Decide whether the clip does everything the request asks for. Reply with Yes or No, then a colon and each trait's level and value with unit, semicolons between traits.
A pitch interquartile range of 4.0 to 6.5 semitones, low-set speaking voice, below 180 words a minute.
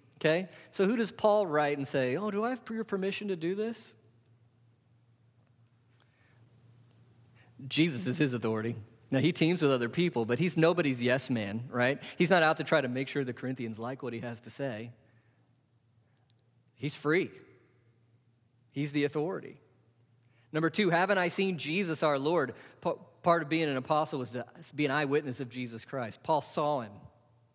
Yes: average, 5.1 semitones; low, 130 Hz; average, 170 wpm